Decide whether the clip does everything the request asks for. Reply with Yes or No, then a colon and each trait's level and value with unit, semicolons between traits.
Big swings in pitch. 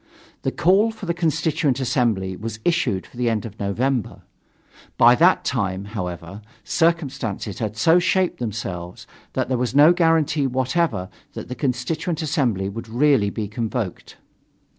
Yes: wide, 7.1 semitones